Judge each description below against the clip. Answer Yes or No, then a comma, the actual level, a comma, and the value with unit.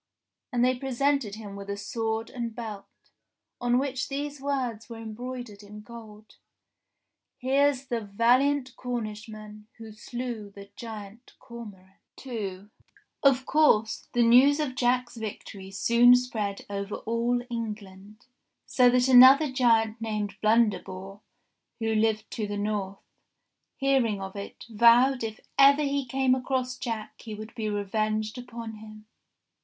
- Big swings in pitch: No, average, 3.0 semitones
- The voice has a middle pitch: No, high, 230 Hz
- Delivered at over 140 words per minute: No, slow, 135 wpm